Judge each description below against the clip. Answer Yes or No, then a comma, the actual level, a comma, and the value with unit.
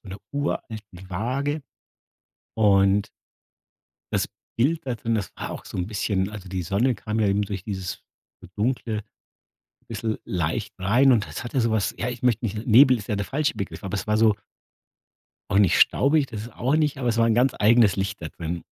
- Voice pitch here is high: No, low, 110 Hz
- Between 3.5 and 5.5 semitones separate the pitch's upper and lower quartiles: Yes, average, 3.9 semitones